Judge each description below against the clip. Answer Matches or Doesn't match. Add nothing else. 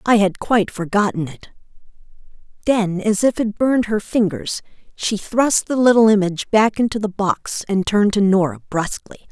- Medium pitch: Doesn't match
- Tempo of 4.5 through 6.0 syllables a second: Matches